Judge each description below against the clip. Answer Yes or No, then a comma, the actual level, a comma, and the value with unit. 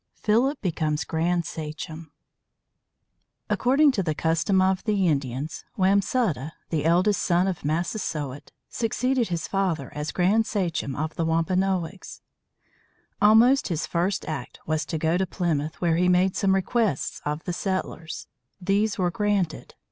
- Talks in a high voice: No, medium, 180 Hz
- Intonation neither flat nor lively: Yes, average, 3.8 semitones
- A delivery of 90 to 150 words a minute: Yes, average, 140 wpm